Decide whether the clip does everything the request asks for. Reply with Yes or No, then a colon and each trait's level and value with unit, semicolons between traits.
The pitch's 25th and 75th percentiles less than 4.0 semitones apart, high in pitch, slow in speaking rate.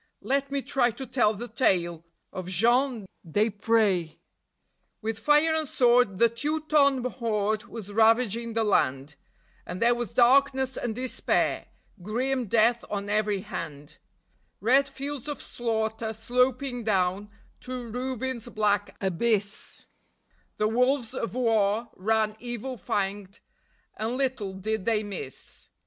Yes: average, 3.6 semitones; high, 230 Hz; slow, 125 wpm